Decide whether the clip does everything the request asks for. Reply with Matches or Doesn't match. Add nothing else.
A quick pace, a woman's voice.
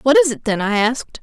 Matches